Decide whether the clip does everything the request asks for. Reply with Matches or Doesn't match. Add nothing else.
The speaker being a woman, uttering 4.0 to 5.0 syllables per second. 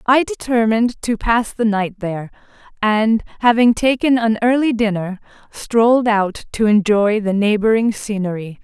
Matches